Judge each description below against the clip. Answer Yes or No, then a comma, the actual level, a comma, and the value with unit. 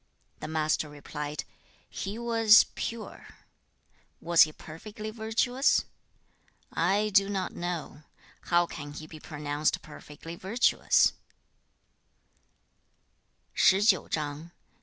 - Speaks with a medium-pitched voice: Yes, medium, 175 Hz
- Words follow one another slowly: Yes, slow, 85 wpm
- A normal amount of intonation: No, wide, 5.7 semitones